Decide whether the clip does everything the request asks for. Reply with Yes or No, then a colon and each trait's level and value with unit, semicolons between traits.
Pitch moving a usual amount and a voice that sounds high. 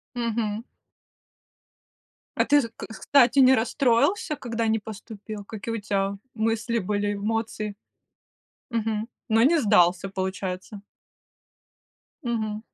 No: narrow, 2.2 semitones; high, 220 Hz